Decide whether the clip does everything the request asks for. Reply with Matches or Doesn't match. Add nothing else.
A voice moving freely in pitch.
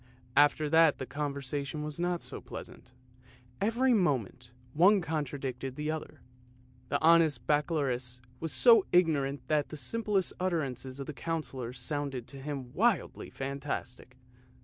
Doesn't match